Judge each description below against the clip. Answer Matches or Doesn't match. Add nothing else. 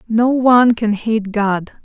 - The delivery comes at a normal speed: Matches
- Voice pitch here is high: Matches